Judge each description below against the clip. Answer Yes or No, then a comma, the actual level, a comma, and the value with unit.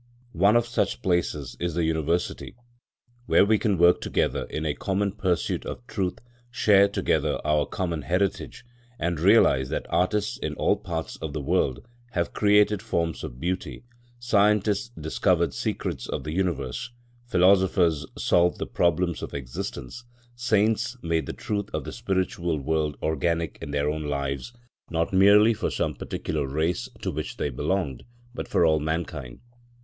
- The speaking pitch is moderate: No, very low, 85 Hz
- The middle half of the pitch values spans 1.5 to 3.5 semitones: No, average, 4.5 semitones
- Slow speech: No, average, 155 wpm